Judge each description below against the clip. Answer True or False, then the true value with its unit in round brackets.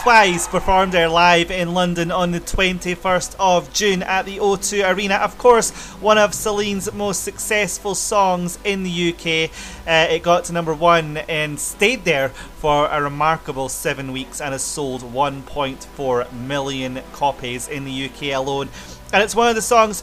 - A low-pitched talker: False (170 Hz)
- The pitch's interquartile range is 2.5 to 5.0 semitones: False (5.5 semitones)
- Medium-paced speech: True (170 wpm)